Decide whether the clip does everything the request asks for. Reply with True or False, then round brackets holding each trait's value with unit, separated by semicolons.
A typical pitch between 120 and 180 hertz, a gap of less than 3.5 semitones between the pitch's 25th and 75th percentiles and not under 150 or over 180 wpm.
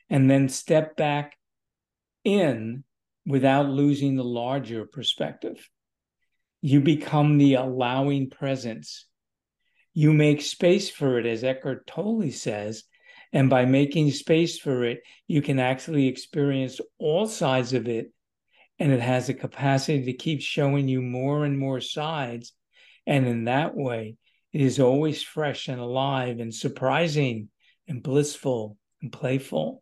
False (135 Hz; 2.5 semitones; 135 wpm)